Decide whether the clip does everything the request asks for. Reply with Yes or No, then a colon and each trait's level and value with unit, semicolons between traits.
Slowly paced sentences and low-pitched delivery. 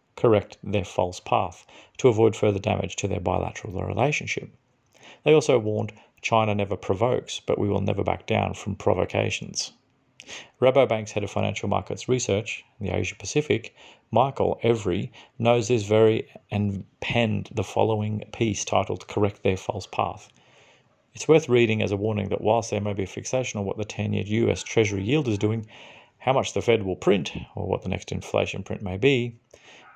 No: average, 175 wpm; low, 105 Hz